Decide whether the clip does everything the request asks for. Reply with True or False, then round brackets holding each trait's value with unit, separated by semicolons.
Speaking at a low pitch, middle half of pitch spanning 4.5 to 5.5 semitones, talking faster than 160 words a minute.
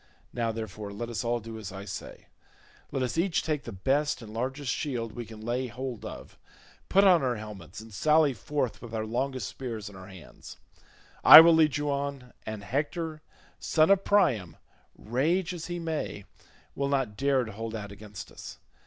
True (125 Hz; 5.2 semitones; 190 wpm)